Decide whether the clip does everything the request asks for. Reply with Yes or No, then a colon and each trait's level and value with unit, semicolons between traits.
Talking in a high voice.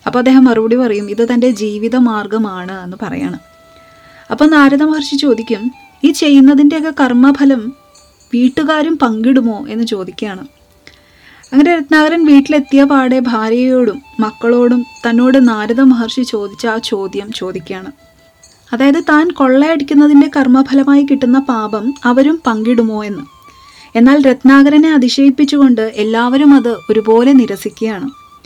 Yes: very high, 255 Hz